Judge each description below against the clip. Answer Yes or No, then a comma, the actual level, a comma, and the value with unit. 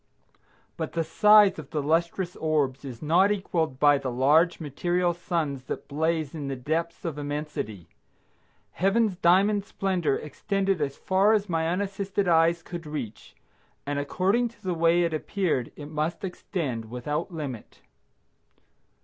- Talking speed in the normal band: Yes, average, 145 wpm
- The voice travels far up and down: No, average, 4.3 semitones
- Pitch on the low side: No, medium, 165 Hz